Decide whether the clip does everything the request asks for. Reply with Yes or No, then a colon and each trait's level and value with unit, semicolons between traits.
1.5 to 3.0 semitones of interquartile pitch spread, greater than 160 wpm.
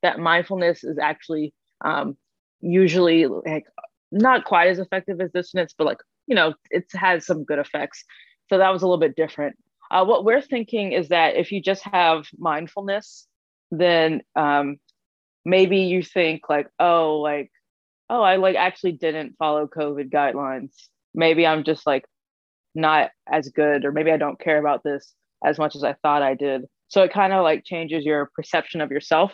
No: average, 3.7 semitones; average, 180 wpm